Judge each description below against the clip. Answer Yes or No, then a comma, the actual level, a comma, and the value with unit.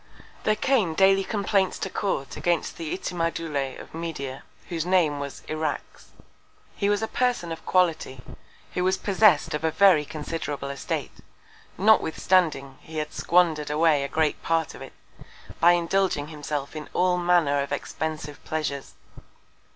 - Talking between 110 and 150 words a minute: Yes, average, 145 wpm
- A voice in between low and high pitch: Yes, medium, 165 Hz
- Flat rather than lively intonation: No, average, 3.6 semitones